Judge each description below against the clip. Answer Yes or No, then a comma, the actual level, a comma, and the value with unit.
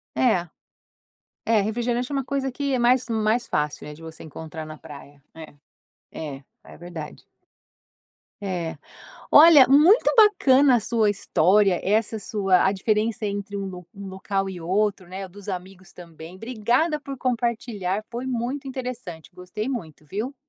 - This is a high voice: Yes, high, 210 Hz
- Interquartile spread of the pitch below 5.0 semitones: No, wide, 5.4 semitones